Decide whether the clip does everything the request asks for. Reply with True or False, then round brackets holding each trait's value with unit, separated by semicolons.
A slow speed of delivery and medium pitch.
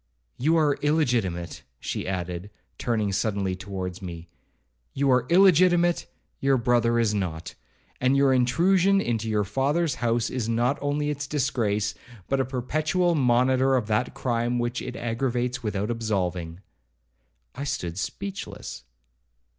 False (130 wpm; 120 Hz)